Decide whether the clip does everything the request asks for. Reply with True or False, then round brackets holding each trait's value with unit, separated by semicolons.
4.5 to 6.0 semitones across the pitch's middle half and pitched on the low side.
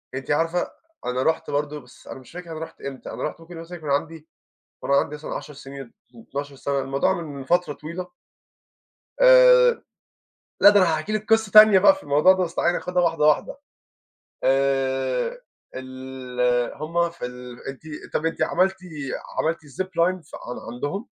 False (4.8 semitones; 155 Hz)